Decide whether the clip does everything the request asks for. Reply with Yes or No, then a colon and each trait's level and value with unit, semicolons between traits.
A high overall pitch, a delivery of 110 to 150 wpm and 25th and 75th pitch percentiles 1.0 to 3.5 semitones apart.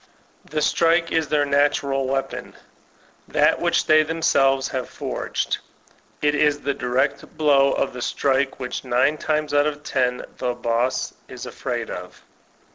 No: medium, 140 Hz; average, 145 wpm; narrow, 2.4 semitones